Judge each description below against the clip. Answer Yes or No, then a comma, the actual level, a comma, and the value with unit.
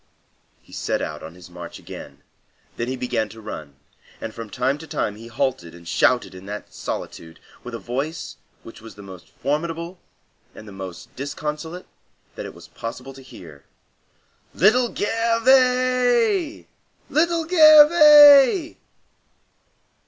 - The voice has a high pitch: No, medium, 140 Hz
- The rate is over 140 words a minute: No, slow, 135 wpm